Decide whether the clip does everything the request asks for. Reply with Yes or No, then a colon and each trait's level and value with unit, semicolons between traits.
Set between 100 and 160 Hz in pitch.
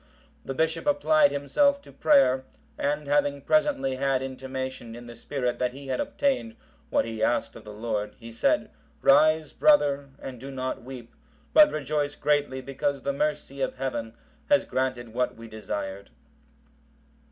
Yes: low, 135 Hz